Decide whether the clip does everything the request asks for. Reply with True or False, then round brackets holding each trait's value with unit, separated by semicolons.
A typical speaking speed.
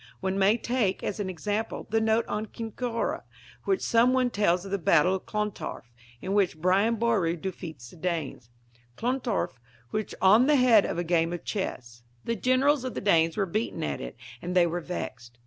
True (190 wpm)